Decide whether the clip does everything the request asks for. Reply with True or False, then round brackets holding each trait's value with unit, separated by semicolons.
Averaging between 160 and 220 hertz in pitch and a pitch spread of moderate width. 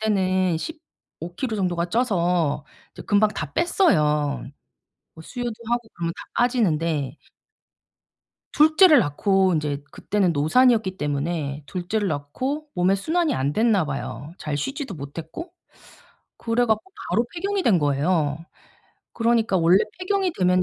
False (185 Hz; 7.6 semitones)